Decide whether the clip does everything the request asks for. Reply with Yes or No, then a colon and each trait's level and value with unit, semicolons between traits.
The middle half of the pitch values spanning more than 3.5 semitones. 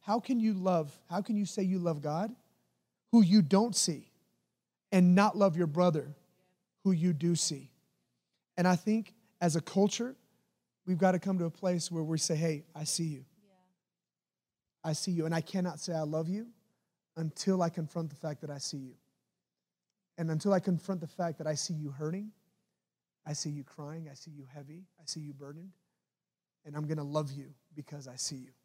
Yes: average, 4.0 semitones